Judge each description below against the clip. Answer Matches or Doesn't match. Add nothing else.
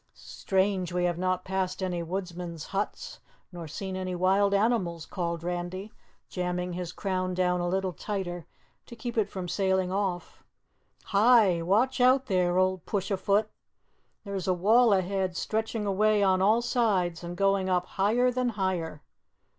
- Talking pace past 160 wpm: Doesn't match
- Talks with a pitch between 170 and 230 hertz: Matches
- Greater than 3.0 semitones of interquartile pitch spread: Doesn't match